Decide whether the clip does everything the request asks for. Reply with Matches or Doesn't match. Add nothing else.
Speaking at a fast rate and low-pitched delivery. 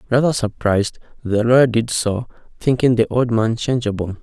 Doesn't match